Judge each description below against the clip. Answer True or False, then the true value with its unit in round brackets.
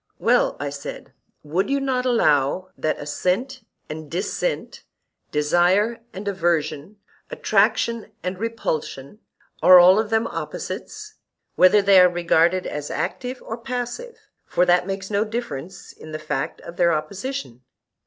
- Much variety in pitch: True (6.1 semitones)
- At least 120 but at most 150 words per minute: True (135 wpm)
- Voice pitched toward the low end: False (185 Hz)